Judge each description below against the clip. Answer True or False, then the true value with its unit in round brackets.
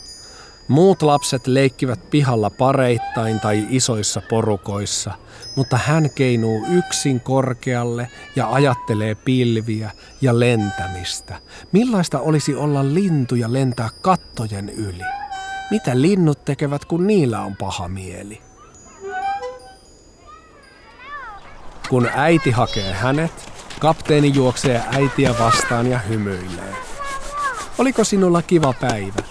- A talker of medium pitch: False (130 Hz)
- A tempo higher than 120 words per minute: False (100 wpm)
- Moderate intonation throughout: False (5.9 semitones)